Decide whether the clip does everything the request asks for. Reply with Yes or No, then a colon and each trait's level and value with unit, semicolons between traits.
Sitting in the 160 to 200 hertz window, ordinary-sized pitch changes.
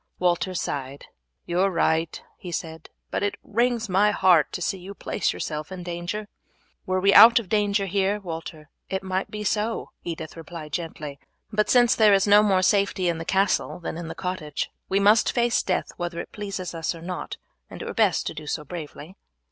Yes: medium, 185 Hz; average, 3.6 semitones